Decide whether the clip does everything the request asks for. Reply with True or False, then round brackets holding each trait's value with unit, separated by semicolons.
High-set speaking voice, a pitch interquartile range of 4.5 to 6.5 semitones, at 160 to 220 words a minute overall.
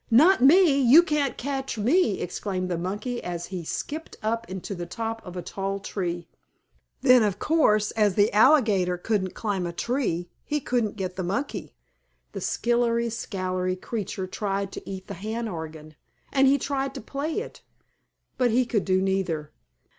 True (210 Hz; 5.3 semitones; 170 wpm)